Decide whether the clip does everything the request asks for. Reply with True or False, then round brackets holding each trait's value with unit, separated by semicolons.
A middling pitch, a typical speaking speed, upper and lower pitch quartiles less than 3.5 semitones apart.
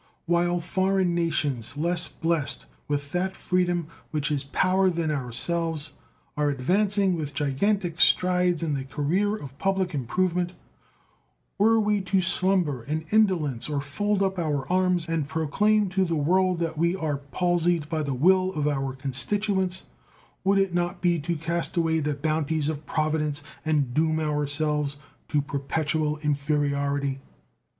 False (160 Hz; 145 wpm; 3.9 semitones)